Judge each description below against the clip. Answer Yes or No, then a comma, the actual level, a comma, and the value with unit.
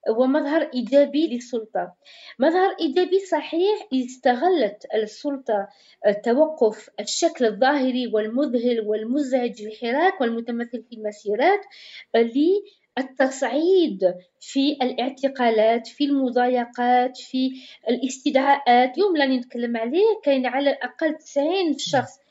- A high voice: Yes, very high, 260 Hz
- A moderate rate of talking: Yes, average, 90 wpm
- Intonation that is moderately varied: Yes, average, 4.1 semitones